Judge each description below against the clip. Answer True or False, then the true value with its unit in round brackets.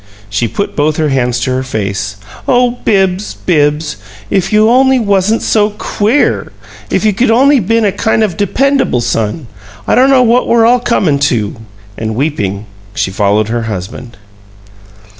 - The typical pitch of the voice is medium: True (180 Hz)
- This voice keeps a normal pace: True (160 wpm)